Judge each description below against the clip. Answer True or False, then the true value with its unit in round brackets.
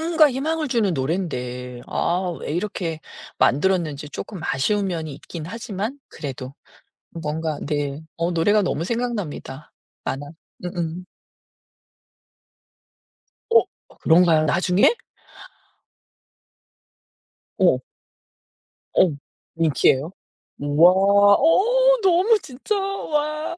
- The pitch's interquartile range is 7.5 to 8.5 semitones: True (8.1 semitones)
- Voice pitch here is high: False (180 Hz)